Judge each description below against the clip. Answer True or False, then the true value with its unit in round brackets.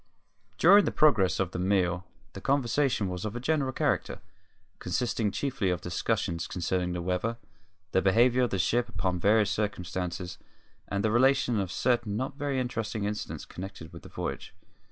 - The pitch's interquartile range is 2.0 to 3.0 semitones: False (5.0 semitones)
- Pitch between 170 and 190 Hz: False (105 Hz)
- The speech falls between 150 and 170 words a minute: True (165 wpm)